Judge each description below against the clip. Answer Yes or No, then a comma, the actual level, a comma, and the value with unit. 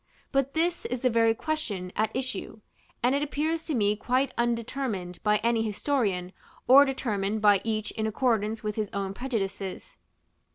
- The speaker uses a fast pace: No, average, 160 wpm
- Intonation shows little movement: No, average, 4.3 semitones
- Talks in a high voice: Yes, high, 225 Hz